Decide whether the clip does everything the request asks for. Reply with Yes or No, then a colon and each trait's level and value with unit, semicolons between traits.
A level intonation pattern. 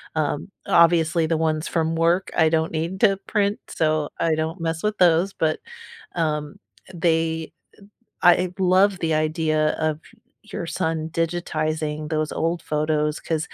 Yes: narrow, 1.8 semitones